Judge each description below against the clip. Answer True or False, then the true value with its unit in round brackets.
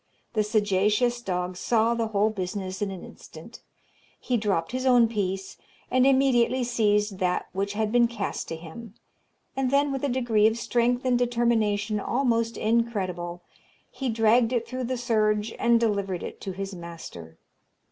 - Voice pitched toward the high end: True (220 Hz)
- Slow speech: False (160 wpm)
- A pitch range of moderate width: True (3.4 semitones)